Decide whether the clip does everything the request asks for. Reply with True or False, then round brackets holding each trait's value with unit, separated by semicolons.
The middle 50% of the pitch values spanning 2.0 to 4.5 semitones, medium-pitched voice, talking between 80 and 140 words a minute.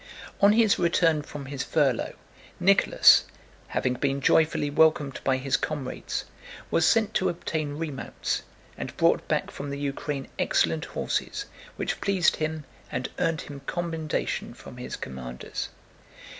True (3.2 semitones; 150 Hz; 135 wpm)